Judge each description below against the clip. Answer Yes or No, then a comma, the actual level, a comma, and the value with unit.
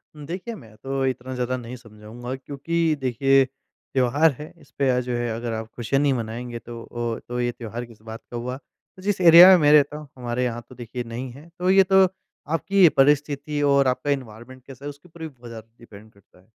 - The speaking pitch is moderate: No, low, 130 Hz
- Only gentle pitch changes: No, average, 3.6 semitones